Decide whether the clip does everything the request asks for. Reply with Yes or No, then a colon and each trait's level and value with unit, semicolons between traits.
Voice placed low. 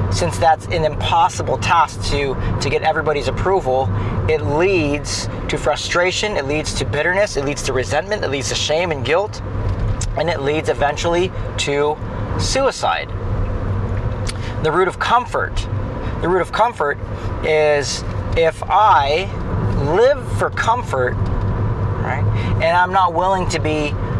Yes: low, 110 Hz